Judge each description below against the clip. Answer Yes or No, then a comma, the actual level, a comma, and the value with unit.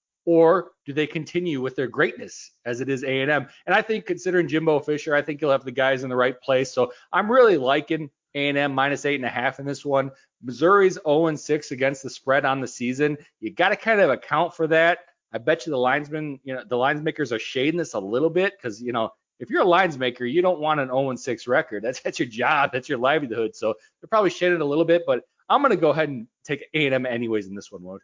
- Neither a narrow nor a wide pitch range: Yes, average, 4.0 semitones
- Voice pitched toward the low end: No, medium, 145 Hz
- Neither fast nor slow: No, fast, 240 wpm